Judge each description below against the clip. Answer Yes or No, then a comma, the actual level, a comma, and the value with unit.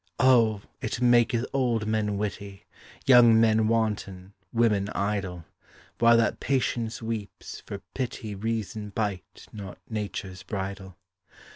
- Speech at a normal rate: No, slow, 115 wpm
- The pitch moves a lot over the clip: No, narrow, 2.5 semitones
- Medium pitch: No, low, 110 Hz